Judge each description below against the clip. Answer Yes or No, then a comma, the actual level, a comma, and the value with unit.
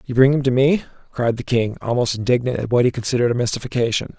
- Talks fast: Yes, fast, 230 wpm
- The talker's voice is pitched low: Yes, low, 125 Hz